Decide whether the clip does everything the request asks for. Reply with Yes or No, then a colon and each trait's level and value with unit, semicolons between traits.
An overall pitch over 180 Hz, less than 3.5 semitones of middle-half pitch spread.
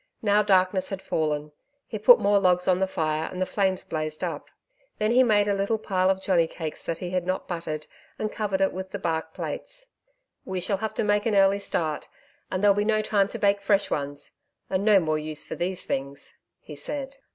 No: high, 190 Hz; average, 4.0 semitones